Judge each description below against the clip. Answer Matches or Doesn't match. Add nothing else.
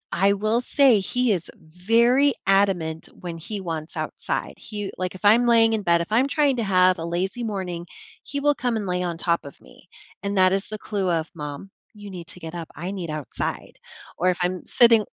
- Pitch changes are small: Doesn't match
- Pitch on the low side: Doesn't match